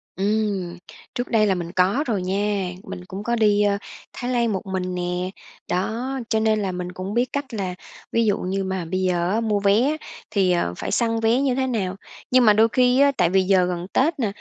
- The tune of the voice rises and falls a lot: No, average, 4.0 semitones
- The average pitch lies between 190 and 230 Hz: Yes, high, 205 Hz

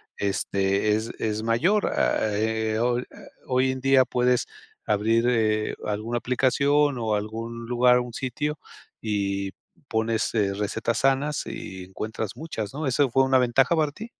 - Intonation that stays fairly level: No, average, 3.5 semitones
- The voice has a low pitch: Yes, low, 115 Hz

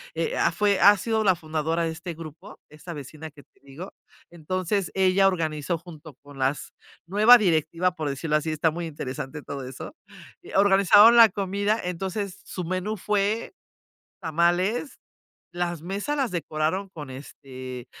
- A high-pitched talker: No, medium, 175 Hz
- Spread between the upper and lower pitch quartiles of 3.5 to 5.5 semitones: Yes, average, 4.3 semitones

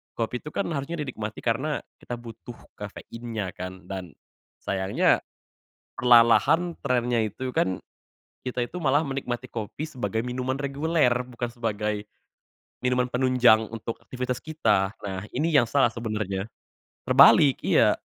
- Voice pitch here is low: Yes, low, 120 Hz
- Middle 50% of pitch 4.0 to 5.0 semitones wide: No, average, 3.3 semitones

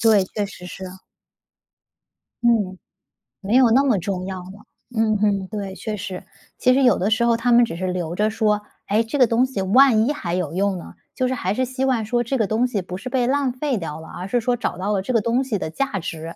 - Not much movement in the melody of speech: No, average, 4.5 semitones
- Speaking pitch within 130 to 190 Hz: No, high, 215 Hz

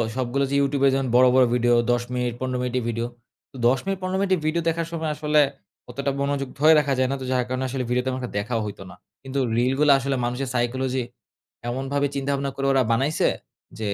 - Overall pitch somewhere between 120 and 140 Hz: Yes, low, 135 Hz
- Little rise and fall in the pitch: Yes, narrow, 2.1 semitones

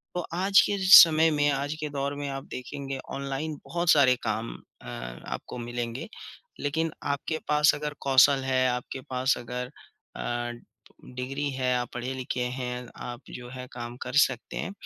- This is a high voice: No, low, 135 Hz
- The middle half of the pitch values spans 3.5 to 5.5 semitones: No, average, 2.8 semitones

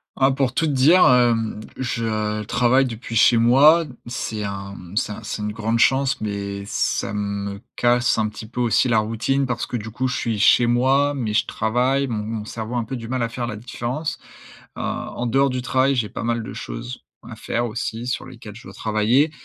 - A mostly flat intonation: No, average, 3.2 semitones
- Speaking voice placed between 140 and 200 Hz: No, low, 120 Hz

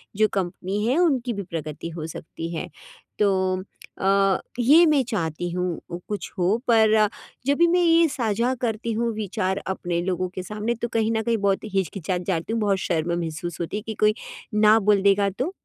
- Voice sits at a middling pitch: No, high, 200 Hz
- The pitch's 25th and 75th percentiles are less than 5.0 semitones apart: Yes, average, 4.0 semitones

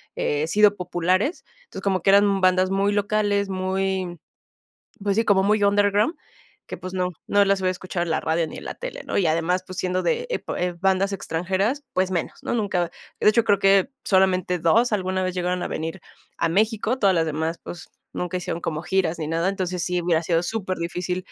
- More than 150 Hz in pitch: Yes, medium, 185 Hz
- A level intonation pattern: Yes, narrow, 2.3 semitones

